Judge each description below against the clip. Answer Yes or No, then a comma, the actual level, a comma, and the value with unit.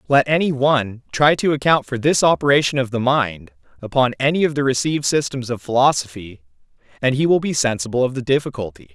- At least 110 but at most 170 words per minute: No, average, 190 wpm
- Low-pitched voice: Yes, low, 130 Hz